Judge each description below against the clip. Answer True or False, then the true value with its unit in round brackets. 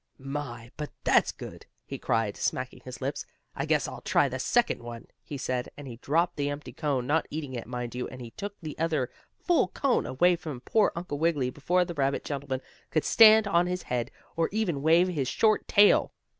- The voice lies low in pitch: False (145 Hz)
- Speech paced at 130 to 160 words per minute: False (205 wpm)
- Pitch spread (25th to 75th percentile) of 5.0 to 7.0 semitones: True (5.3 semitones)